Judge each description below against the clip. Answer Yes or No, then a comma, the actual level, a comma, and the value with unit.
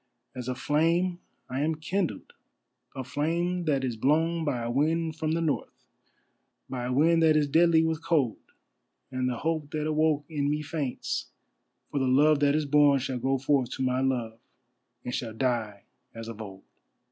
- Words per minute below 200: Yes, average, 180 wpm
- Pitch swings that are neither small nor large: Yes, average, 3.8 semitones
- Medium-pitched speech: Yes, medium, 145 Hz